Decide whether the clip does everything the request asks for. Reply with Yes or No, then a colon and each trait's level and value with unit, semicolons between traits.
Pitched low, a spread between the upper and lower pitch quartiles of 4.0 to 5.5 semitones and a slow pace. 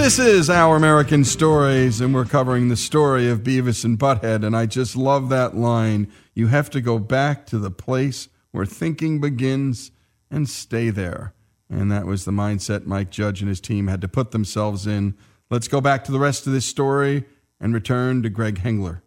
No: low, 120 Hz; average, 4.6 semitones; average, 200 wpm